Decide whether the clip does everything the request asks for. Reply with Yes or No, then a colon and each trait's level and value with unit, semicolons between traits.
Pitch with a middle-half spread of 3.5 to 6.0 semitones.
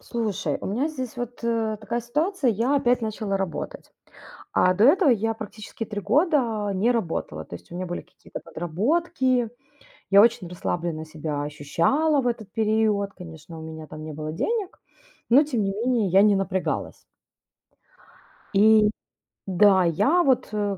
Yes: average, 5.3 semitones